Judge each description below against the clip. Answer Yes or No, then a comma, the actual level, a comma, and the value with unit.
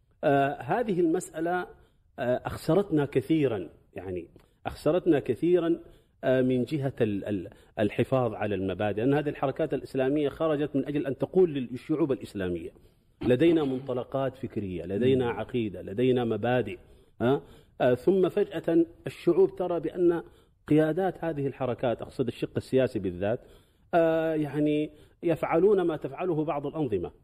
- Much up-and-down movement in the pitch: No, average, 4.8 semitones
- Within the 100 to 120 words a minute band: Yes, average, 105 wpm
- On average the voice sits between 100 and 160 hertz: Yes, medium, 140 Hz